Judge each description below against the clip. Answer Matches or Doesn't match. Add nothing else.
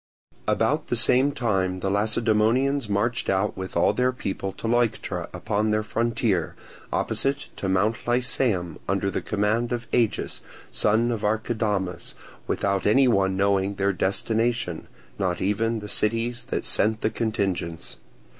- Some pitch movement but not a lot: Matches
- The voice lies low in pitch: Matches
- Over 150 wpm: Doesn't match